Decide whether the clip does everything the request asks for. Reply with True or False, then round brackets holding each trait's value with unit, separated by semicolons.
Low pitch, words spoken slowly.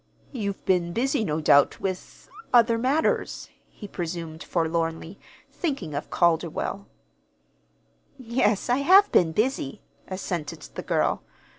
False (190 Hz; 115 wpm)